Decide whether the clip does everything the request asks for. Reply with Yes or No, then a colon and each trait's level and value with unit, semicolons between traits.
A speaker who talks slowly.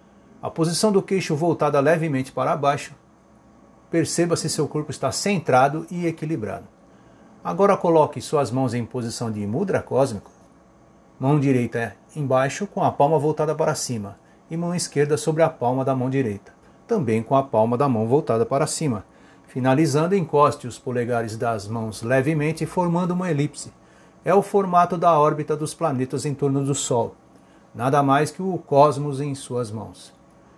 No: average, 160 wpm